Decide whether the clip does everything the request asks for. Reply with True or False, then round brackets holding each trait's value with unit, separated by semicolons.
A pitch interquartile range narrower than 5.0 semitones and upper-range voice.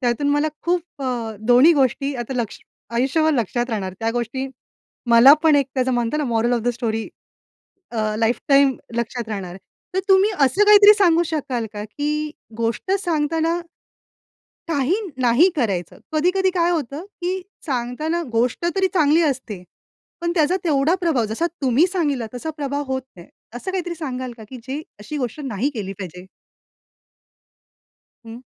False (5.4 semitones; 270 Hz)